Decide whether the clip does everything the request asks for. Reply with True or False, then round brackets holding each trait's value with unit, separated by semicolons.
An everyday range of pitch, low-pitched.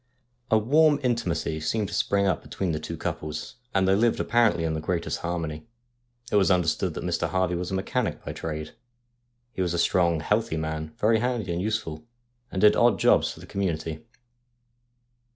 True (4.8 semitones; 90 Hz)